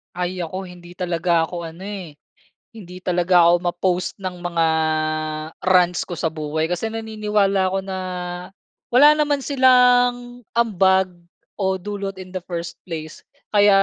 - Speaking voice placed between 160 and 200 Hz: Yes, medium, 185 Hz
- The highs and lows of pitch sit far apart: No, average, 3.0 semitones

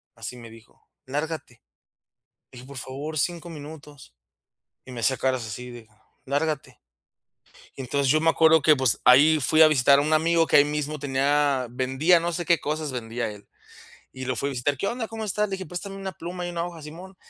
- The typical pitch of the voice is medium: Yes, medium, 145 Hz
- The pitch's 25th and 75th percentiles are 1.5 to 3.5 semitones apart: No, average, 4.0 semitones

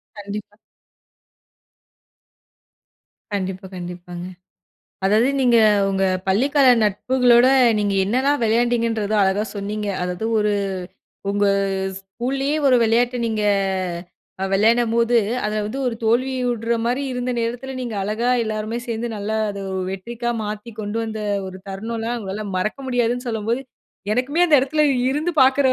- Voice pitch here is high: Yes, high, 225 Hz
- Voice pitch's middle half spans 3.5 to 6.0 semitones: No, average, 3.1 semitones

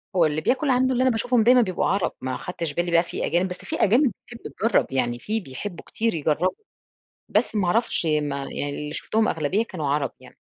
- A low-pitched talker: No, medium, 180 Hz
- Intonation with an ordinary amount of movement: No, wide, 7.1 semitones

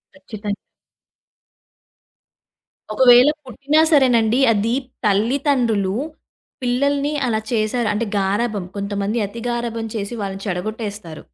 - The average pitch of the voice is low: No, high, 225 Hz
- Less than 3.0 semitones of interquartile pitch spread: No, average, 3.3 semitones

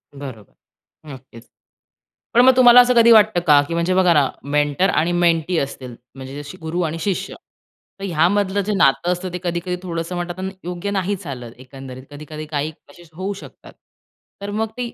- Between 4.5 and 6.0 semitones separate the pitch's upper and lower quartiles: Yes, average, 4.8 semitones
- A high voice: No, medium, 170 Hz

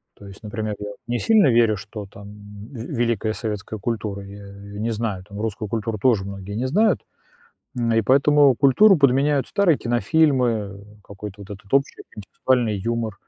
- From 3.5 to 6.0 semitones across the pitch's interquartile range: Yes, average, 3.9 semitones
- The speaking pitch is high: No, low, 110 Hz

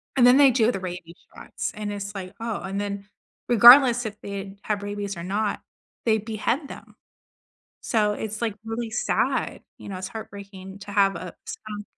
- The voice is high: Yes, high, 205 Hz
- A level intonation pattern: Yes, narrow, 2.2 semitones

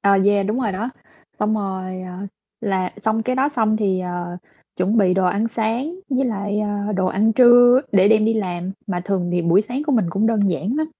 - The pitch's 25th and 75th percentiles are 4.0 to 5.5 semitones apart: No, average, 3.3 semitones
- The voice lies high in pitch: Yes, high, 205 Hz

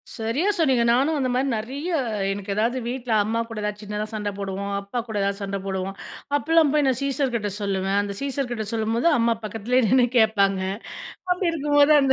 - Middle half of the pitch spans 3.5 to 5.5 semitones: Yes, average, 5.0 semitones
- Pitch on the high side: Yes, high, 230 Hz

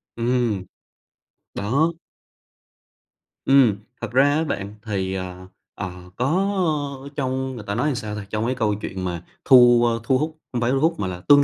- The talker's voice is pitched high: No, low, 120 Hz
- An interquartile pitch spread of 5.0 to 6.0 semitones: Yes, average, 5.3 semitones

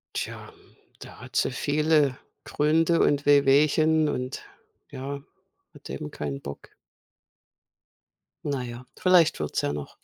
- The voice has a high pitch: No, medium, 140 Hz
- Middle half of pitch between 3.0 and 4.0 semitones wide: Yes, average, 3.6 semitones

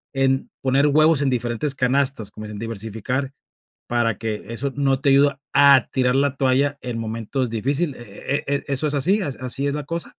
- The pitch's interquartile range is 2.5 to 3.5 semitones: Yes, average, 3.1 semitones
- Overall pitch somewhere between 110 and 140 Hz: Yes, low, 135 Hz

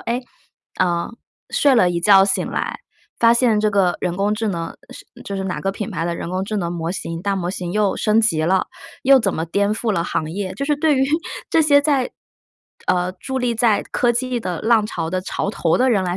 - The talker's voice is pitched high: Yes, high, 200 Hz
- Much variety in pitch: No, average, 4.8 semitones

